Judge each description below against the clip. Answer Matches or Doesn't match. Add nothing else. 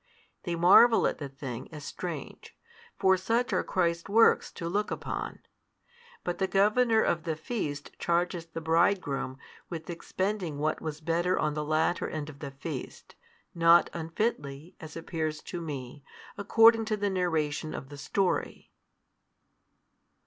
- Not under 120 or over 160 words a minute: Matches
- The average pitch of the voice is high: Doesn't match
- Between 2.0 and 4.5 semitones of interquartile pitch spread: Matches